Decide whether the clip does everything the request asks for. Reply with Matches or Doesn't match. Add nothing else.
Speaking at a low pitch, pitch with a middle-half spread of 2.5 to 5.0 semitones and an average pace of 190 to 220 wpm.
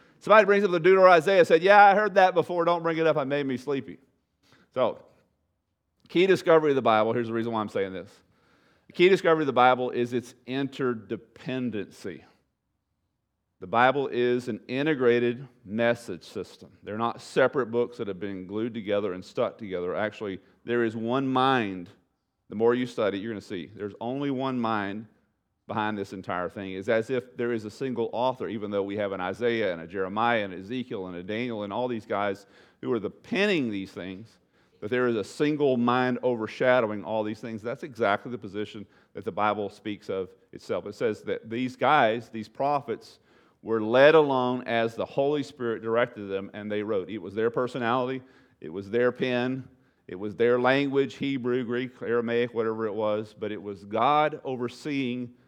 Matches